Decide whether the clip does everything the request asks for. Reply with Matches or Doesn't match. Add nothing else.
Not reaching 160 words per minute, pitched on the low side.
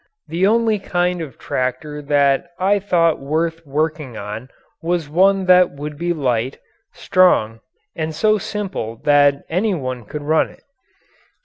Doesn't match